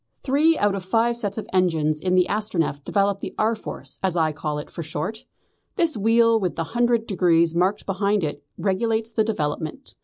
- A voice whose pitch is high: Yes, high, 195 Hz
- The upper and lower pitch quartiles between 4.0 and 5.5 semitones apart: Yes, average, 5.1 semitones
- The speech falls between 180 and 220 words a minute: Yes, average, 195 wpm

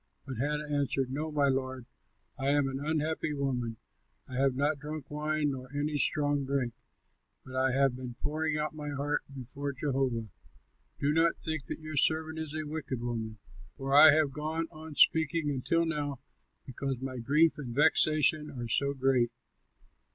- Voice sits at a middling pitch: Yes, medium, 145 Hz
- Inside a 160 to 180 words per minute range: Yes, average, 165 wpm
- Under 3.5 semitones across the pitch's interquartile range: Yes, average, 2.7 semitones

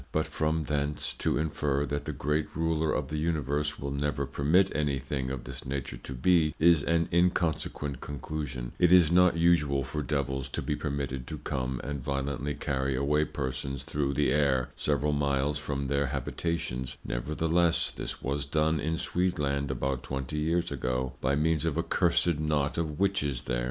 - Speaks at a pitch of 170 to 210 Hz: No, very low, 75 Hz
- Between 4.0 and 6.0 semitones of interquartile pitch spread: No, narrow, 2.5 semitones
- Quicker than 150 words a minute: Yes, average, 175 wpm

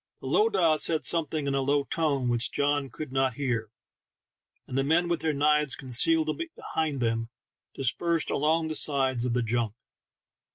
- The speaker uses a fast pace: No, average, 165 wpm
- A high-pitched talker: No, medium, 140 Hz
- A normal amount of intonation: Yes, average, 3.7 semitones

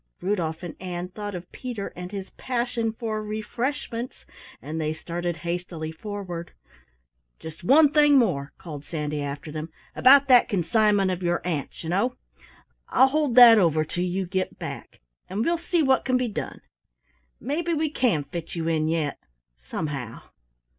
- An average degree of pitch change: No, wide, 6.9 semitones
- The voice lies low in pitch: No, medium, 185 Hz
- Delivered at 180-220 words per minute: No, average, 160 wpm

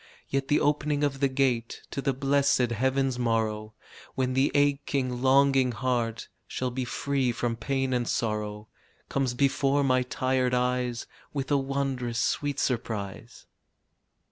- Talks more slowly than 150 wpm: Yes, average, 140 wpm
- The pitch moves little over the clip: Yes, narrow, 2.3 semitones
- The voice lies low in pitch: Yes, low, 130 Hz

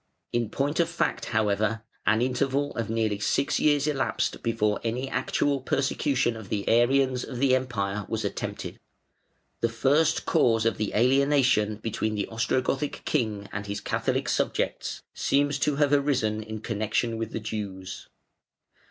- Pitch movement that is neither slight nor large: Yes, average, 4.2 semitones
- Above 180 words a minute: No, average, 145 wpm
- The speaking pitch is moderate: No, low, 115 Hz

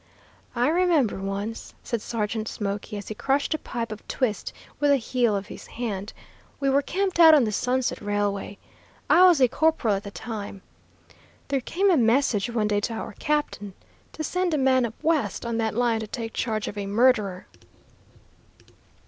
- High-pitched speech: Yes, high, 235 Hz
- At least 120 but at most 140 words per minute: No, average, 180 wpm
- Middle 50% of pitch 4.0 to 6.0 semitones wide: Yes, average, 5.0 semitones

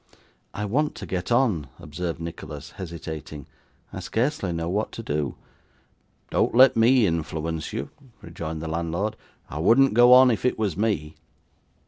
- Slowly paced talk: No, average, 150 wpm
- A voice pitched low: Yes, very low, 85 Hz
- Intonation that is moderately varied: No, wide, 6.1 semitones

